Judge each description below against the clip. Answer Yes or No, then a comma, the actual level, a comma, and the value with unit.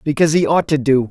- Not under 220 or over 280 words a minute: Yes, fast, 270 wpm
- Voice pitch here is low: No, medium, 145 Hz